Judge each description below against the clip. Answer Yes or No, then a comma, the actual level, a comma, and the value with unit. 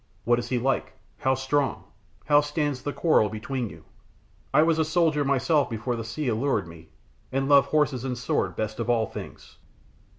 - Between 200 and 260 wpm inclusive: No, average, 185 wpm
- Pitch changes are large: No, average, 3.9 semitones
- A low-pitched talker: Yes, low, 130 Hz